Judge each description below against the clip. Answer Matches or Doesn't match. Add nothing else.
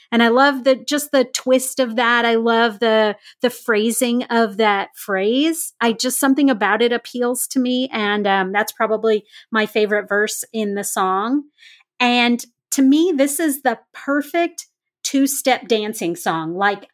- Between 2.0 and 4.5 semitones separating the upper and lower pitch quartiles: Matches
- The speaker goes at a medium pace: Matches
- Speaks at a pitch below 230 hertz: Doesn't match